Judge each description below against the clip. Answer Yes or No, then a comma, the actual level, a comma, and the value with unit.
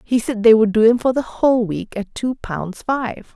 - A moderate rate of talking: No, fast, 250 wpm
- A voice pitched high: Yes, high, 230 Hz